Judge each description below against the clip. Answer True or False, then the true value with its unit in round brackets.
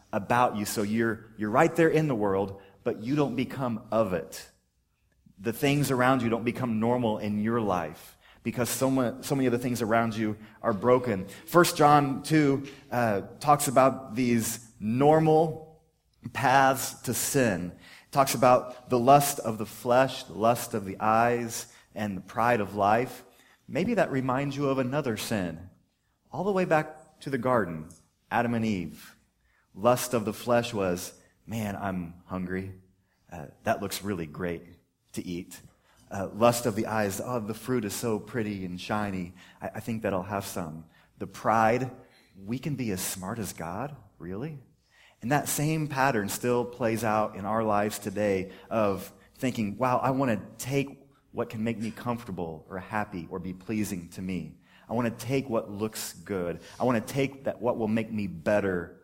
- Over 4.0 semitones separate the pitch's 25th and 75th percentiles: True (4.4 semitones)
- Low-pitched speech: True (115 Hz)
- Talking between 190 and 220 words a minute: False (175 wpm)